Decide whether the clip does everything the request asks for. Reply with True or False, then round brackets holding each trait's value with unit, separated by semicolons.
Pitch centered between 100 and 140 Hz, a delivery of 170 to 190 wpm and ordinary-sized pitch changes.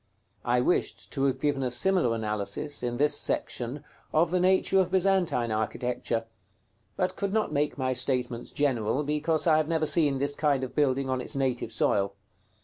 True (135 Hz; 175 wpm; 4.2 semitones)